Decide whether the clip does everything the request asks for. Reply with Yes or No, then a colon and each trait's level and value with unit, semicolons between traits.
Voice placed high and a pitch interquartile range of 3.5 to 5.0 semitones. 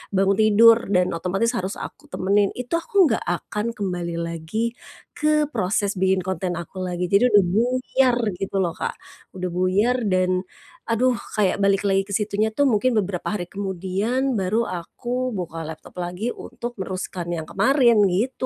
Yes: high, 195 Hz; average, 3.9 semitones